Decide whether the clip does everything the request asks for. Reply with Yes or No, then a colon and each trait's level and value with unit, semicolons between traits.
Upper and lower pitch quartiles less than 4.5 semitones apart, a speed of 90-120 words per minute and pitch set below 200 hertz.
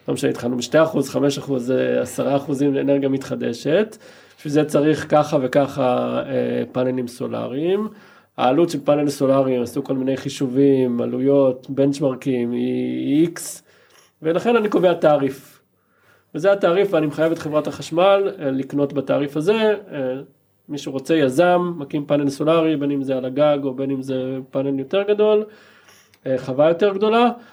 No: average, 3.5 semitones; average, 140 wpm; medium, 140 Hz